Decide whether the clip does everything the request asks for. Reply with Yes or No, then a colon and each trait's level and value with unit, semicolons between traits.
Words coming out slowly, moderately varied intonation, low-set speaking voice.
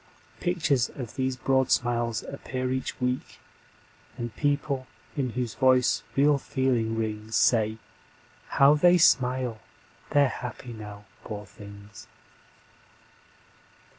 Yes: slow, 105 wpm; average, 3.2 semitones; low, 125 Hz